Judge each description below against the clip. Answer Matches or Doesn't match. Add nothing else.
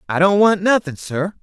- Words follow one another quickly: Matches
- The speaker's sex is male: Matches